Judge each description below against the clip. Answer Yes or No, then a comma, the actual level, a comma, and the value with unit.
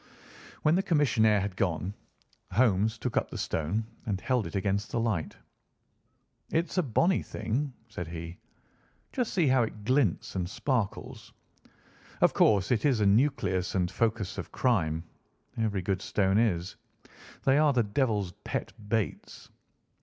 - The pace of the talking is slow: No, average, 145 wpm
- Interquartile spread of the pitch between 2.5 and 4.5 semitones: No, average, 5.2 semitones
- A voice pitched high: No, low, 110 Hz